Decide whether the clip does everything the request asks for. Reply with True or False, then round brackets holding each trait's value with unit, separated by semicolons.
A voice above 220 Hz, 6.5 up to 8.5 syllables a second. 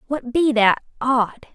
False (250 Hz; 3.5 syllables/s)